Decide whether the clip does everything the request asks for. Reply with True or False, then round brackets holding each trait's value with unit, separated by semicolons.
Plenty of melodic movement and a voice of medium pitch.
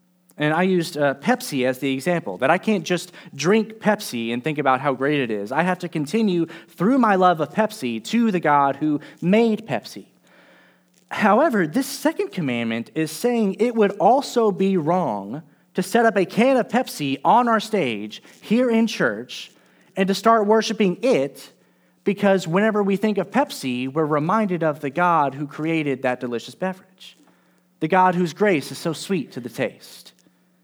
True (6.7 semitones; 180 Hz)